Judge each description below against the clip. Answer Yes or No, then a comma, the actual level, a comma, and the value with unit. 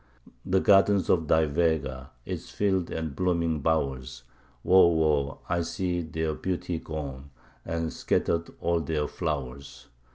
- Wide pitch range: No, average, 3.1 semitones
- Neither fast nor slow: No, slow, 130 wpm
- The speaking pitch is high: No, very low, 80 Hz